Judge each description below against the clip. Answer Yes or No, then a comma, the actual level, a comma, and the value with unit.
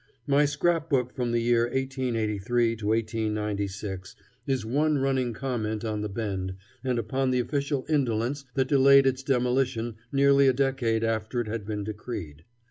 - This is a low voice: Yes, low, 120 Hz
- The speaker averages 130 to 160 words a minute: Yes, average, 155 wpm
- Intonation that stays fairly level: No, average, 3.8 semitones